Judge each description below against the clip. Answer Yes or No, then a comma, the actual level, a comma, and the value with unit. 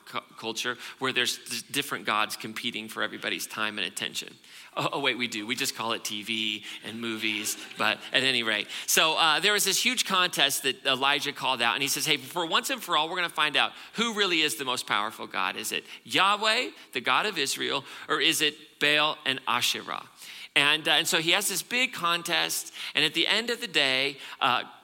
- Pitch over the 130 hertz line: Yes, medium, 140 Hz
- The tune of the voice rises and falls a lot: Yes, wide, 7.0 semitones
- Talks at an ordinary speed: No, fast, 215 wpm